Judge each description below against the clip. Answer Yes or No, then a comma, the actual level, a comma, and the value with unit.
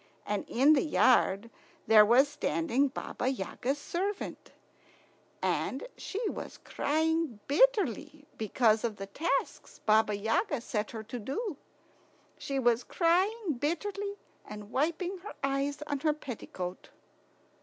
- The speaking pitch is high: Yes, very high, 275 Hz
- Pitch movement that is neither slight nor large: No, wide, 6.9 semitones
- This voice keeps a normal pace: No, slow, 125 wpm